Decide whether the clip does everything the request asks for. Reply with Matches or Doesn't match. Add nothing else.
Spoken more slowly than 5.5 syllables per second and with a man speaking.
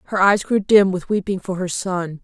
Doesn't match